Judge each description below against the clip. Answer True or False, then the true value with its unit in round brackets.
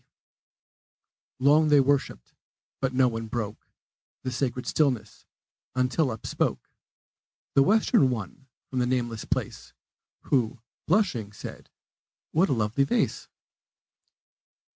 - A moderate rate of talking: False (110 wpm)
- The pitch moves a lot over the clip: False (3.7 semitones)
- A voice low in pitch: True (130 Hz)